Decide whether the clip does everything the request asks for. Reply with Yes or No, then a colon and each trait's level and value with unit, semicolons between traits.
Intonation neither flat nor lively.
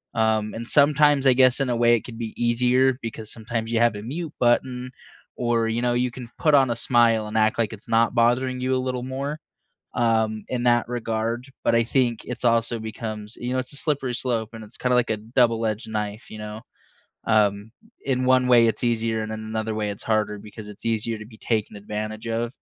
No: narrow, 2.2 semitones